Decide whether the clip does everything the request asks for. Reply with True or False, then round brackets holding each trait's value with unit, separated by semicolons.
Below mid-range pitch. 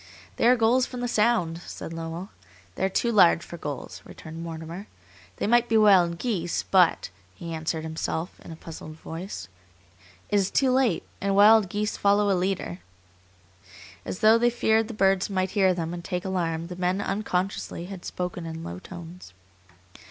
False (185 Hz)